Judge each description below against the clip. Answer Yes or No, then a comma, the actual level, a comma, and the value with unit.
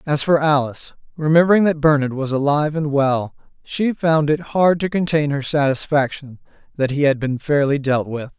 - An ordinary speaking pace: Yes, average, 180 wpm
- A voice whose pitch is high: No, medium, 145 Hz